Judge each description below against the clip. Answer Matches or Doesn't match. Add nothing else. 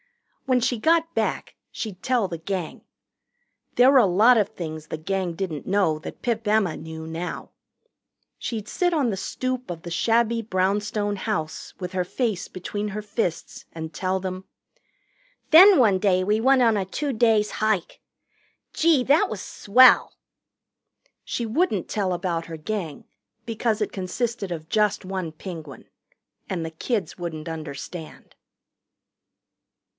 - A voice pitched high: Matches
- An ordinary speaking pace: Matches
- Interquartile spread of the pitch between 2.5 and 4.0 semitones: Doesn't match